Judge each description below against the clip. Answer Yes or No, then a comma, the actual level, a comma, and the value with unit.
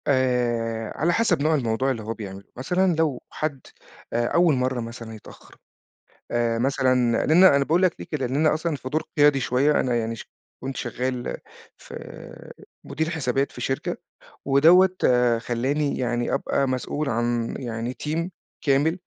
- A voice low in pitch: Yes, low, 130 Hz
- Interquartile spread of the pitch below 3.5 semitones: No, average, 4.2 semitones